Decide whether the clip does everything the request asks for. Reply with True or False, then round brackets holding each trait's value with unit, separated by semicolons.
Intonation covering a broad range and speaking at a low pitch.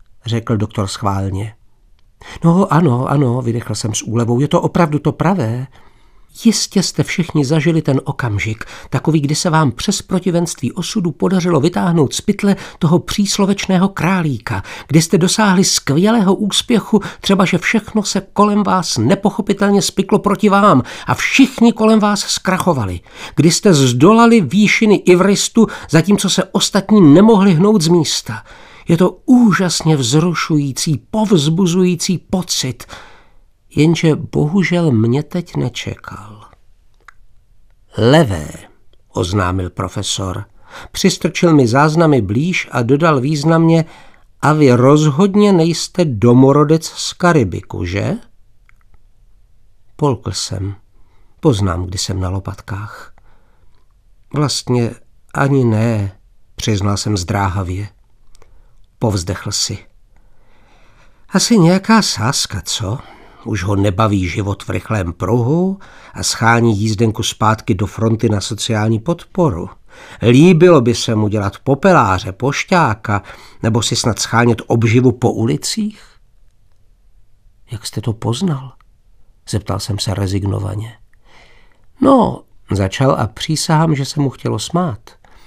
True (9.0 semitones; 130 Hz)